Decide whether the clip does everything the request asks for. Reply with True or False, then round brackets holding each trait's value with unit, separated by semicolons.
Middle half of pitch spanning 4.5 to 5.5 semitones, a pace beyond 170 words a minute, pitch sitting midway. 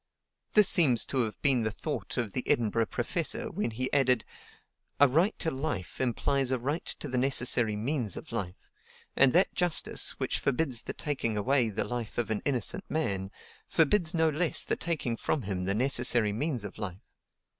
False (5.1 semitones; 180 wpm; 125 Hz)